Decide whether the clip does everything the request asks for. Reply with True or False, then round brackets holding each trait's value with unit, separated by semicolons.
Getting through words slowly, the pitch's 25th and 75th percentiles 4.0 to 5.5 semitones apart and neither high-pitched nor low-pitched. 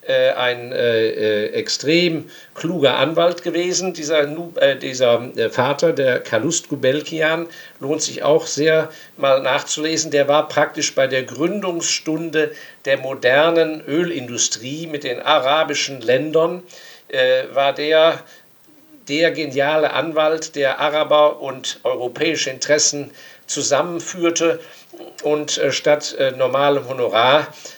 False (110 wpm; 2.7 semitones; 160 Hz)